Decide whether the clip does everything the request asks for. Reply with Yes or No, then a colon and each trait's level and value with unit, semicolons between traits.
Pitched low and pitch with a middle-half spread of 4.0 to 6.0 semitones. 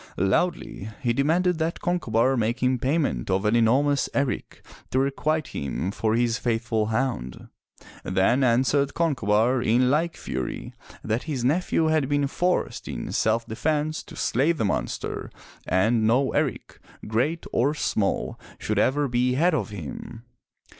Yes: low, 125 Hz; average, 4.8 semitones